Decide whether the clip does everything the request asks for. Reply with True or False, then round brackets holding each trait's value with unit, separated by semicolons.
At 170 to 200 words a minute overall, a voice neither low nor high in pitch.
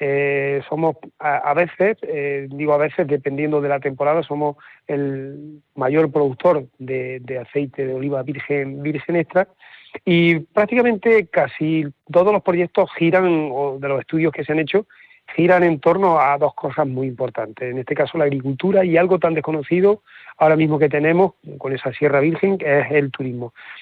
True (175 wpm; 150 Hz)